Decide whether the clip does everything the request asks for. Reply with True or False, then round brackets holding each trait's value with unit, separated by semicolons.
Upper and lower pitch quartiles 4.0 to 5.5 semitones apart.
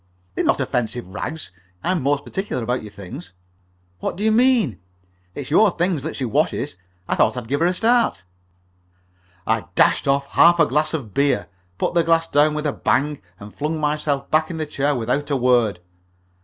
True (4.8 semitones)